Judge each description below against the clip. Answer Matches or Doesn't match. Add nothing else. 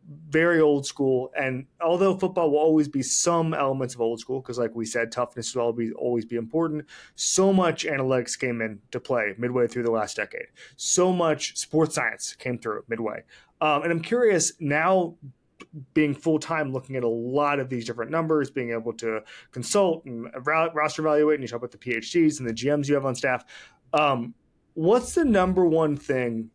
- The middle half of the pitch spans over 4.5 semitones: Matches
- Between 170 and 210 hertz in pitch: Doesn't match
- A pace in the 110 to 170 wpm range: Doesn't match